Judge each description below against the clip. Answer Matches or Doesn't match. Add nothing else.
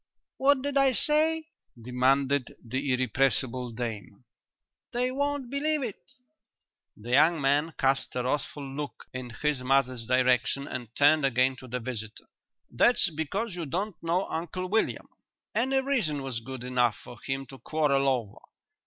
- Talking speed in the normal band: Matches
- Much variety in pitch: Matches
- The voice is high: Doesn't match